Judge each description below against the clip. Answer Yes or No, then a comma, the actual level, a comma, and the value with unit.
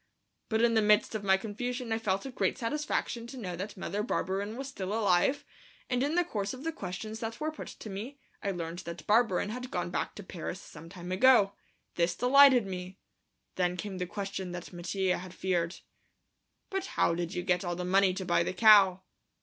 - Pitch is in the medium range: No, high, 200 Hz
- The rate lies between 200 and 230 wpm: Yes, fast, 205 wpm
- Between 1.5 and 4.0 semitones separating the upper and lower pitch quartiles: No, average, 4.4 semitones